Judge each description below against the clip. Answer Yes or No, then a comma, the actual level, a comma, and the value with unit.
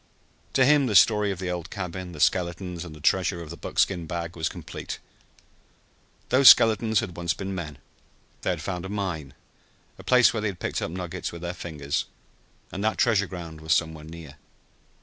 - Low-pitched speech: Yes, very low, 90 Hz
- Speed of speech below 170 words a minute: No, average, 190 wpm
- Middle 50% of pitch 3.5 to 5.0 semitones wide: No, average, 3.1 semitones